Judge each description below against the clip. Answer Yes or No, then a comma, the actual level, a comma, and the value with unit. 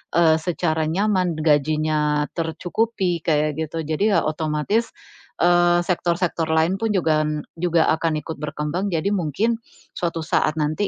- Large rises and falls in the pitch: No, narrow, 2.5 semitones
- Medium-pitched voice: Yes, medium, 165 Hz